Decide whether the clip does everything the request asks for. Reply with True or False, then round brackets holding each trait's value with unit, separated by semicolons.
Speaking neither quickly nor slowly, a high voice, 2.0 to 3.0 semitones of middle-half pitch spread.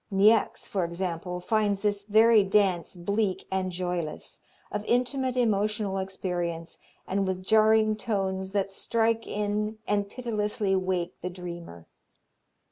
False (125 wpm; 200 Hz; 2.7 semitones)